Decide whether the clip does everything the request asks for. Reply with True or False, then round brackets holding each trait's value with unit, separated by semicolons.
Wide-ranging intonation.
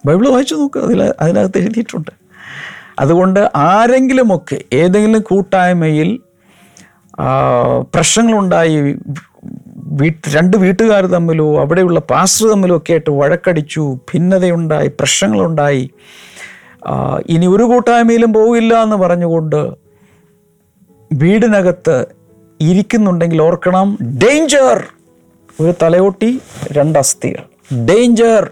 True (5.7 semitones)